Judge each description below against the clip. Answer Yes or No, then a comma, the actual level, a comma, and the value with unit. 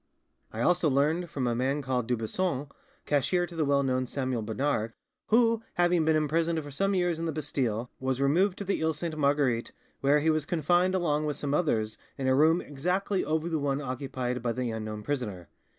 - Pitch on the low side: No, medium, 145 Hz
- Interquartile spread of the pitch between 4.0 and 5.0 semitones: Yes, average, 4.5 semitones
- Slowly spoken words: No, average, 200 wpm